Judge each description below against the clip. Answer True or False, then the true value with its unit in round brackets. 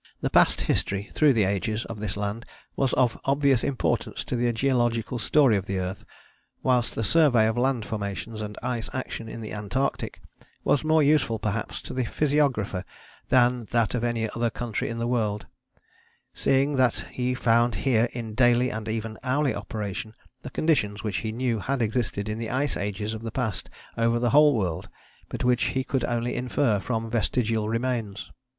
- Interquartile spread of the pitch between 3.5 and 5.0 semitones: False (2.9 semitones)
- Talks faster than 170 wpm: True (180 wpm)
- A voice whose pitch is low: True (115 Hz)